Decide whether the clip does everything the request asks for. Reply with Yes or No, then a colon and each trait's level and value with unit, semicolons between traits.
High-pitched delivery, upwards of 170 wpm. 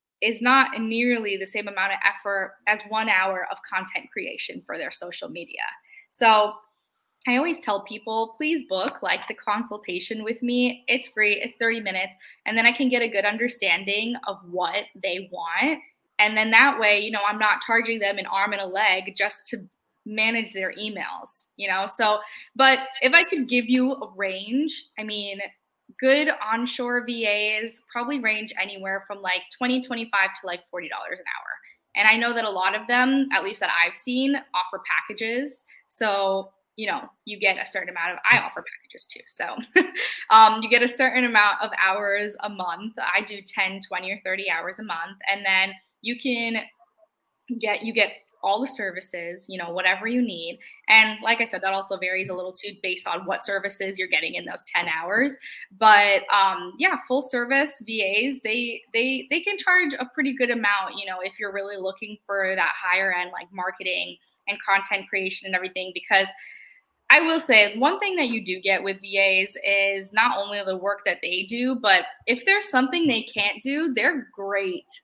Yes: high, 215 Hz; average, 195 wpm